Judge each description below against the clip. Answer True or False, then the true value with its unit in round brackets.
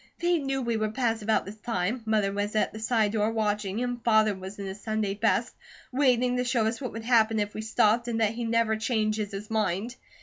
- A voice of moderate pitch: False (220 Hz)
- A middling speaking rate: False (230 wpm)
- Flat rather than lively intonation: True (2.2 semitones)